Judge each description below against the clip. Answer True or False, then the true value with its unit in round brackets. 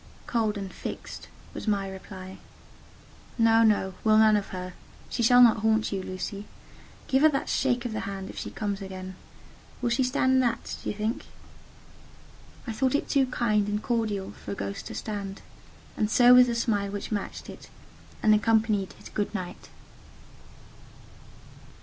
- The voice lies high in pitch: True (215 Hz)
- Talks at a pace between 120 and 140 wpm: False (170 wpm)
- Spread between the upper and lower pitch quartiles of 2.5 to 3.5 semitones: True (3.1 semitones)